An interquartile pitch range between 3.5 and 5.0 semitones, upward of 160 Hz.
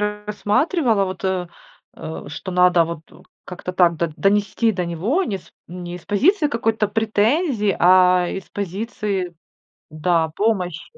No: average, 3.1 semitones; high, 190 Hz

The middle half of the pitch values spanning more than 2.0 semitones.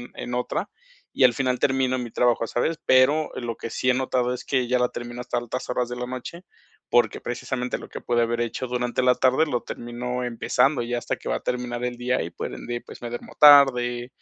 No: narrow, 1.1 semitones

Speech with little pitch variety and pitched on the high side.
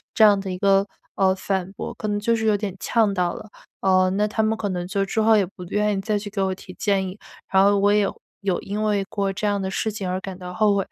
Yes: narrow, 1.7 semitones; high, 200 Hz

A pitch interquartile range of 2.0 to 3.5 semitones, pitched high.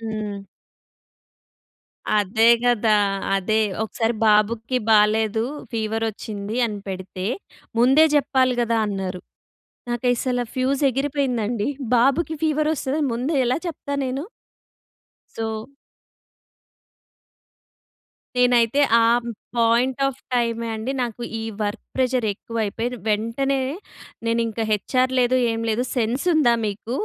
Yes: average, 2.9 semitones; high, 235 Hz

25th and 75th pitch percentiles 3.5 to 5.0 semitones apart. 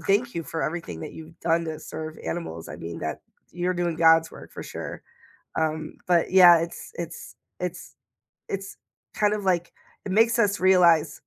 No: average, 2.7 semitones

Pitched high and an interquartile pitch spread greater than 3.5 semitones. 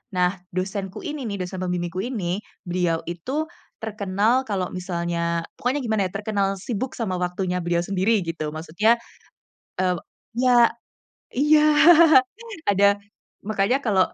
Yes: high, 195 Hz; average, 4.0 semitones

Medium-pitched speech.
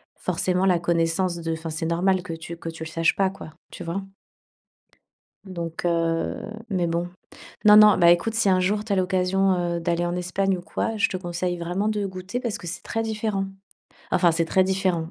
Yes: medium, 180 Hz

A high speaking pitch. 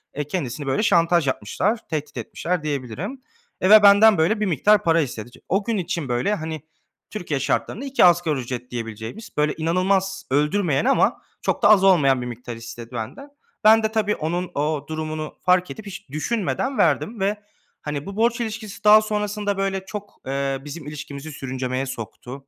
No: medium, 165 Hz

